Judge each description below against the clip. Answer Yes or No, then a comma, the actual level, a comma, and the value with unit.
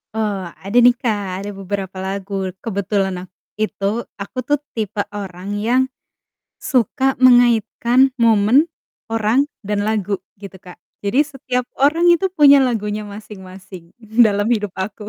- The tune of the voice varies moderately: Yes, average, 3.7 semitones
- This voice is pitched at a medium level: No, high, 210 Hz